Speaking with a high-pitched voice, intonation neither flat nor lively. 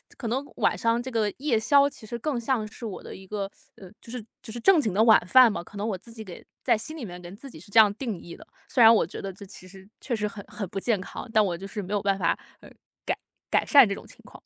Yes: high, 215 Hz; average, 3.3 semitones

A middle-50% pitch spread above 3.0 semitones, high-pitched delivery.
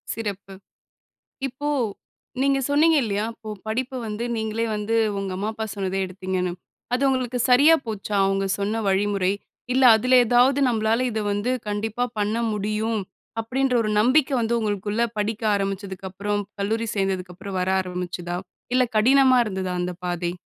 Yes: average, 3.6 semitones; high, 215 Hz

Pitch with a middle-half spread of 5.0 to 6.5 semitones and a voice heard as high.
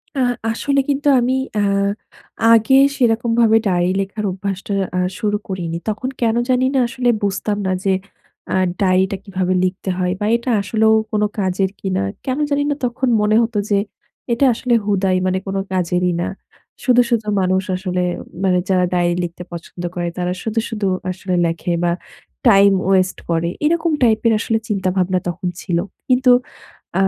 No: average, 4.0 semitones; high, 200 Hz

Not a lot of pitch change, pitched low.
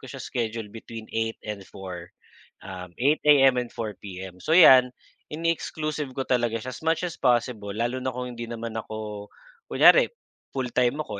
No: average, 3.8 semitones; low, 120 Hz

